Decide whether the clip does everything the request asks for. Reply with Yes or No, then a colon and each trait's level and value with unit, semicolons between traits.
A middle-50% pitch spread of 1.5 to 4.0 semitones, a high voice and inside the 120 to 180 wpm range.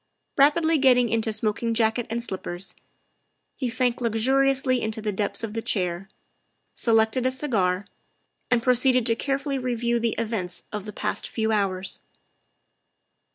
Yes: average, 3.1 semitones; high, 230 Hz; average, 140 wpm